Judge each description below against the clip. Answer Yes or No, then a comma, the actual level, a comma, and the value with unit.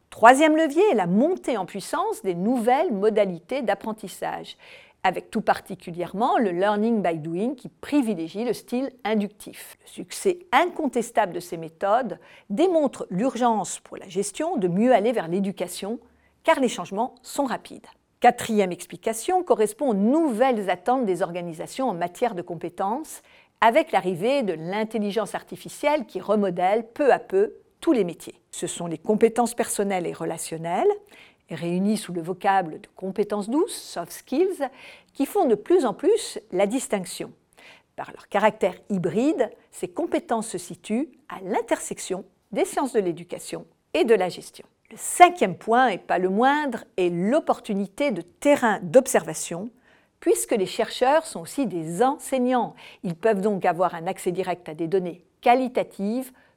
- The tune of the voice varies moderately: No, wide, 6.5 semitones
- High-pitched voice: Yes, high, 225 Hz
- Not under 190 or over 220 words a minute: No, average, 150 wpm